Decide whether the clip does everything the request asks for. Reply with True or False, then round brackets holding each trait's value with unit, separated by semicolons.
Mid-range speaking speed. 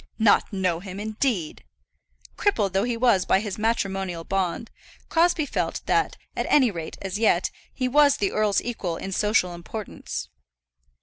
True (150 wpm)